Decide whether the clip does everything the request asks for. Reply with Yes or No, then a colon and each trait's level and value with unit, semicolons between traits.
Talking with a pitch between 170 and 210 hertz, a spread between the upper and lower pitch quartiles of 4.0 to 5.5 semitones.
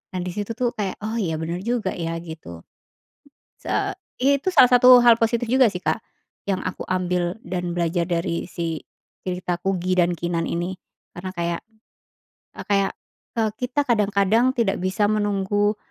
Yes: high, 190 Hz; average, 4.4 semitones